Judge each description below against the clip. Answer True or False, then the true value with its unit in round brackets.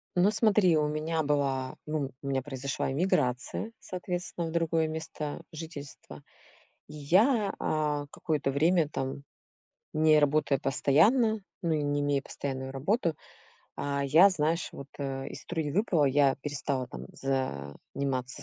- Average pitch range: True (3.3 semitones)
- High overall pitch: False (150 Hz)